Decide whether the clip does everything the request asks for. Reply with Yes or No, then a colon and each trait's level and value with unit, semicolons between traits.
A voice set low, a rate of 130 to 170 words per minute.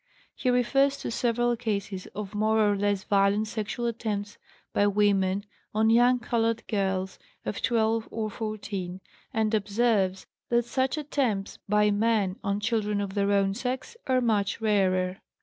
No: high, 215 Hz; average, 150 wpm